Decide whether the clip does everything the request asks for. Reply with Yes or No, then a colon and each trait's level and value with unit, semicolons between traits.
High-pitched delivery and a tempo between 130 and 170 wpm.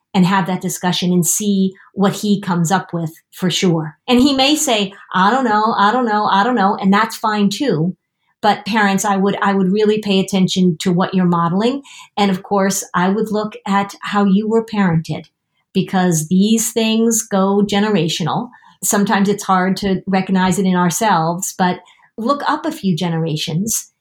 No: high, 195 Hz; average, 180 wpm